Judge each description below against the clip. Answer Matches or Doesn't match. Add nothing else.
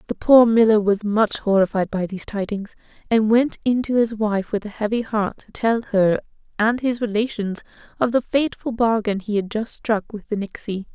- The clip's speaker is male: Doesn't match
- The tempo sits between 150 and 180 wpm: Doesn't match